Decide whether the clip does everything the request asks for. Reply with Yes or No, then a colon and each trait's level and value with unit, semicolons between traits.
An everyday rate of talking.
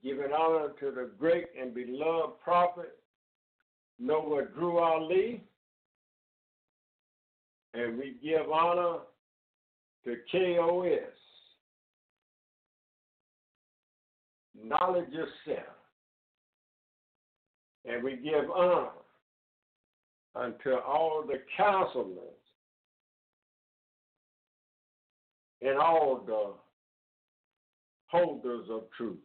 No: slow, 70 wpm